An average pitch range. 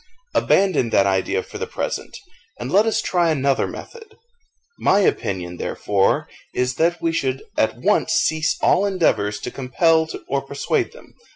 No: wide, 6.8 semitones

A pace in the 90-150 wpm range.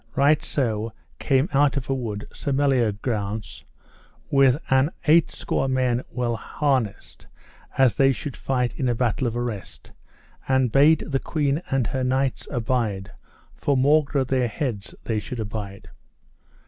Yes: average, 145 wpm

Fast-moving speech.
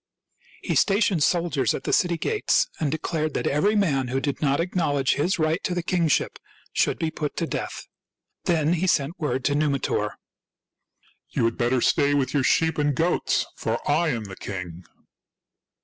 No: average, 180 wpm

